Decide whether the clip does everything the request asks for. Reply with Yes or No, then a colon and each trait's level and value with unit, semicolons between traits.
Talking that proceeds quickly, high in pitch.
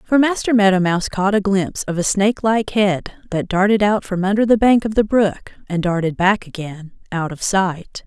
Yes: fast, 210 wpm; high, 195 Hz